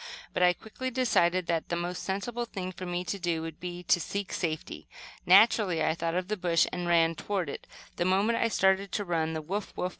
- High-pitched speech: No, medium, 180 Hz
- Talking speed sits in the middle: No, fast, 220 wpm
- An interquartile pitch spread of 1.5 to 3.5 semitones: Yes, average, 2.8 semitones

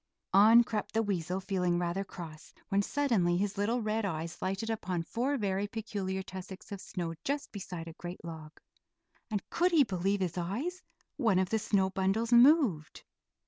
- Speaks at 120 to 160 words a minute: No, average, 170 wpm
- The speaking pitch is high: Yes, high, 195 Hz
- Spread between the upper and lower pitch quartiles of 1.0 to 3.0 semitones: No, average, 3.9 semitones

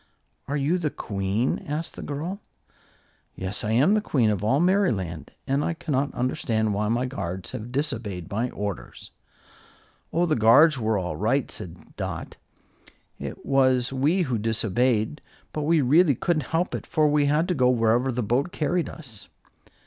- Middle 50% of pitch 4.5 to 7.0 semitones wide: Yes, wide, 5.6 semitones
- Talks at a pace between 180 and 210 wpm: No, average, 165 wpm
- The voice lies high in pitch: No, low, 130 Hz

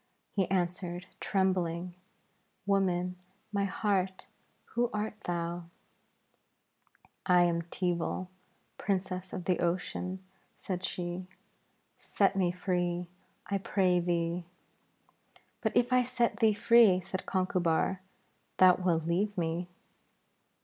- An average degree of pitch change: No, narrow, 1.9 semitones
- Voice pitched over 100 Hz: Yes, medium, 185 Hz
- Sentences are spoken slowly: Yes, slow, 105 wpm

